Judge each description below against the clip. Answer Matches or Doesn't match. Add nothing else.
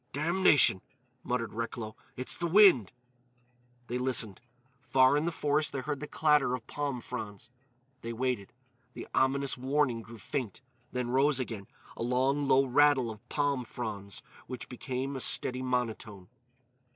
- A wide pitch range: Doesn't match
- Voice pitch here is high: Doesn't match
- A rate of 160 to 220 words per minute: Doesn't match